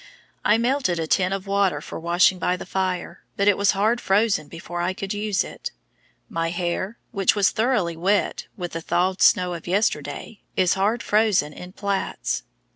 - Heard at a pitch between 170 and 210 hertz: Yes, high, 190 Hz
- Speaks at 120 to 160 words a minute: No, average, 180 wpm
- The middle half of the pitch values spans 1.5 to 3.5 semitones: Yes, average, 2.8 semitones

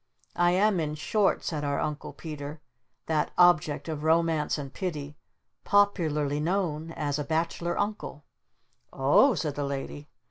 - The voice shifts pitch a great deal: No, average, 2.9 semitones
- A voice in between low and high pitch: Yes, medium, 155 Hz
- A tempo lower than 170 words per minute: Yes, average, 145 wpm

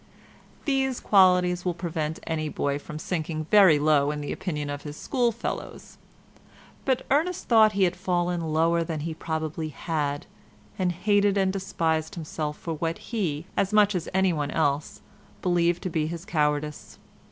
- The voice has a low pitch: No, medium, 170 Hz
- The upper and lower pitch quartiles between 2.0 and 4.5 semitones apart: Yes, average, 3.6 semitones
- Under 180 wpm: Yes, average, 155 wpm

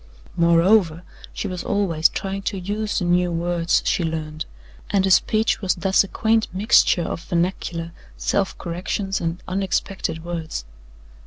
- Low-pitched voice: No, medium, 180 Hz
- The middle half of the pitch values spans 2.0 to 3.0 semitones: Yes, average, 2.7 semitones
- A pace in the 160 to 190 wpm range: No, average, 145 wpm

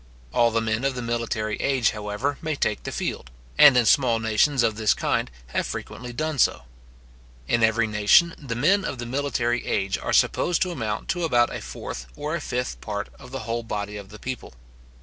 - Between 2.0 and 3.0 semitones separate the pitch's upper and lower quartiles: No, average, 4.0 semitones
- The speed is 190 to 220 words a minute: Yes, fast, 205 wpm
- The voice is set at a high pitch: No, low, 120 Hz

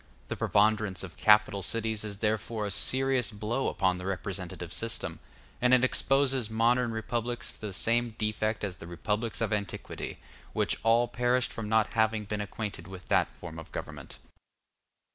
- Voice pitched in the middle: No, low, 110 Hz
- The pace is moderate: Yes, average, 160 wpm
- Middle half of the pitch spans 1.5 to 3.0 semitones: Yes, narrow, 2.5 semitones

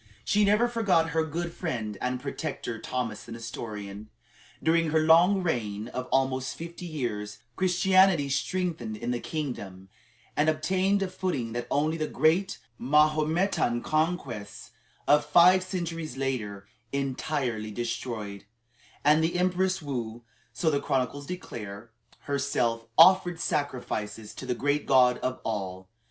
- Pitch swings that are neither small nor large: No, wide, 6.3 semitones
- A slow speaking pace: Yes, slow, 130 wpm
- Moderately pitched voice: Yes, medium, 145 Hz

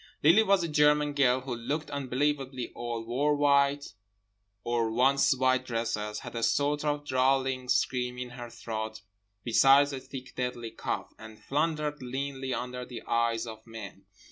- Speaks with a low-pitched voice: Yes, low, 130 Hz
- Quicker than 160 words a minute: No, average, 155 wpm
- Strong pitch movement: No, average, 3.2 semitones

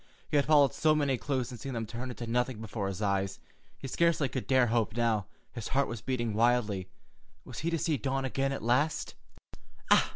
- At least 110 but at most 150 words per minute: No, average, 200 wpm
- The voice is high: No, low, 125 Hz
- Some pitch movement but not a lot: Yes, average, 3.6 semitones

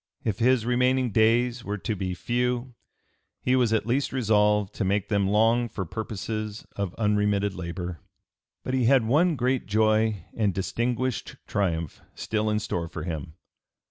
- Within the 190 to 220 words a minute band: No, average, 155 wpm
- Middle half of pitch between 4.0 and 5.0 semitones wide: No, average, 3.5 semitones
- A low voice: Yes, low, 110 Hz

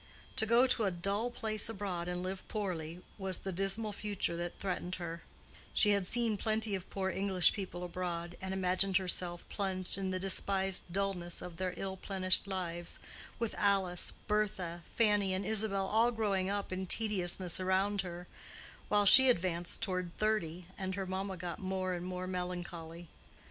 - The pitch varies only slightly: Yes, narrow, 2.1 semitones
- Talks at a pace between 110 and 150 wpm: No, average, 165 wpm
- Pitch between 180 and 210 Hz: Yes, high, 190 Hz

